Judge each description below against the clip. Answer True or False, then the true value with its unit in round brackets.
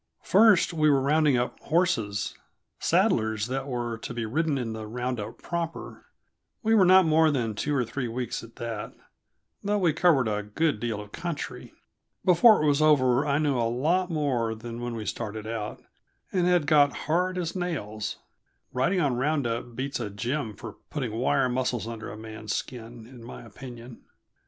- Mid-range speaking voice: False (125 Hz)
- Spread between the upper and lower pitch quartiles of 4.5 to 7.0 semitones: True (5.3 semitones)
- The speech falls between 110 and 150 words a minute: False (180 wpm)